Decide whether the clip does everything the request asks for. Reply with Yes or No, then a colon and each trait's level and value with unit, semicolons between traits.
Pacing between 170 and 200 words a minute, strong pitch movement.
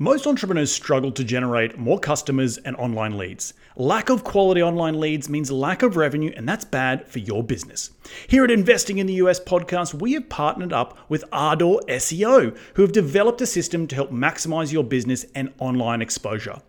Yes: average, 185 wpm; wide, 6.8 semitones